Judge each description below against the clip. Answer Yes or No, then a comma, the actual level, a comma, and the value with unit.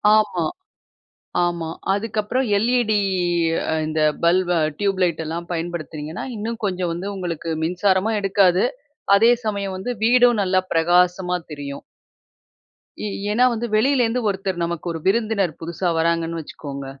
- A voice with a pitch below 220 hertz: Yes, medium, 185 Hz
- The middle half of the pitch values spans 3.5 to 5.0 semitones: Yes, average, 4.1 semitones